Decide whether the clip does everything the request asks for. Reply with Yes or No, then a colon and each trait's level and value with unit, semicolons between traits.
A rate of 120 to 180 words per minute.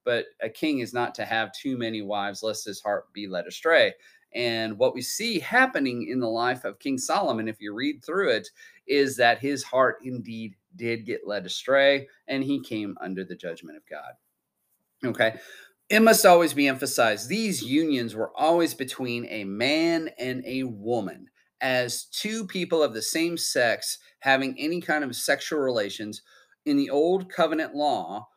Yes: average, 175 wpm